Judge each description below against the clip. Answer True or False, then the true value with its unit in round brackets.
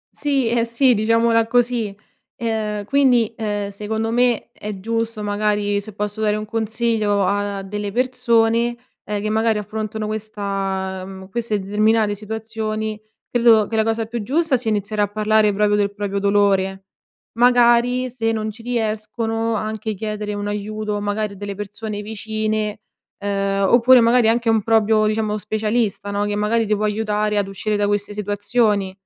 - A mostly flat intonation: True (1.7 semitones)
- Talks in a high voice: True (215 Hz)